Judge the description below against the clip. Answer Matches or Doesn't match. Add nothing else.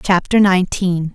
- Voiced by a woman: Matches